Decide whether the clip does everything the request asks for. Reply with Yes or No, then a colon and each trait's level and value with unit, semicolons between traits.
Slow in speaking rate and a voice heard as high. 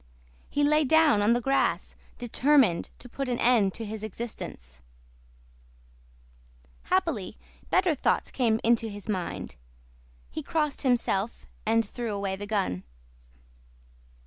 Yes: slow, 120 wpm; high, 225 Hz